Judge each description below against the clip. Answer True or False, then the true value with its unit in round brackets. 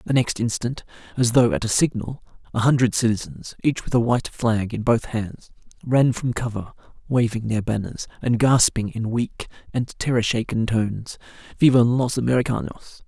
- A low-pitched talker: True (120 Hz)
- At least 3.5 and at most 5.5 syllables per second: True (5.2 syllables/s)